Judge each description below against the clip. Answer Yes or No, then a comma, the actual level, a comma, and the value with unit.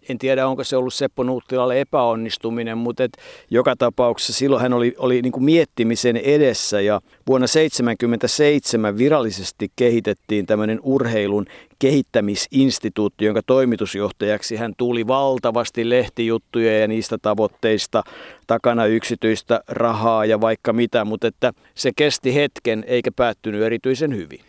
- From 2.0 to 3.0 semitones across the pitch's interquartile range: Yes, average, 2.7 semitones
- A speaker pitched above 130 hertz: No, low, 120 Hz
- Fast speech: No, average, 125 wpm